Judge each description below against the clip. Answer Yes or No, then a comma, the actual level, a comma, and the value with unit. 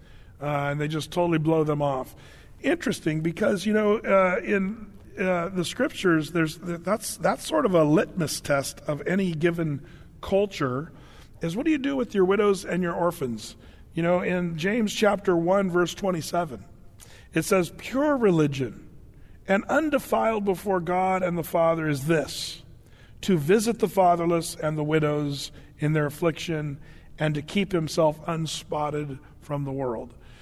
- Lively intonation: No, average, 4.2 semitones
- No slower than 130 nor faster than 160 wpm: Yes, average, 155 wpm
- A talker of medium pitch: Yes, medium, 170 Hz